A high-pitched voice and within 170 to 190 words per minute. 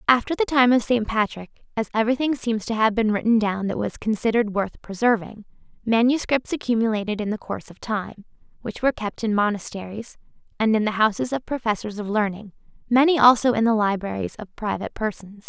Yes: high, 220 Hz; average, 180 wpm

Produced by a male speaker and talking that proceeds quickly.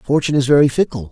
Yes: male; fast, 215 wpm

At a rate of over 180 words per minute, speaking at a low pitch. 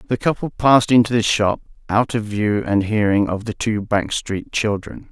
Yes: average, 200 wpm; low, 110 Hz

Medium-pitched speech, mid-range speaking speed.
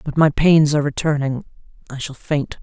Yes: medium, 145 Hz; average, 185 wpm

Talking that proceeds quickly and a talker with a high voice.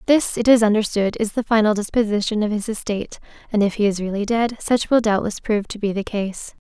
Yes: fast, 225 wpm; high, 215 Hz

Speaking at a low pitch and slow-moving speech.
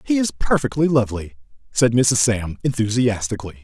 Yes: low, 120 Hz; slow, 130 wpm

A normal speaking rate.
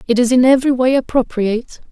Yes: average, 190 wpm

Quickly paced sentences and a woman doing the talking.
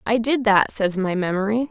Yes: fast, 210 wpm; female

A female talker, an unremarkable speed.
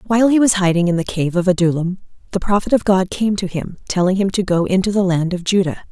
No: female; fast, 255 wpm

